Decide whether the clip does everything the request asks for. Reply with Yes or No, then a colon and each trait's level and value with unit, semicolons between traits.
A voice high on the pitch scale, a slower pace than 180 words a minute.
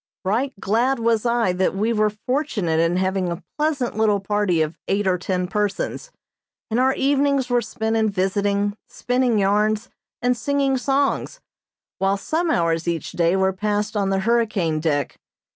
Yes: high, 210 Hz; average, 160 wpm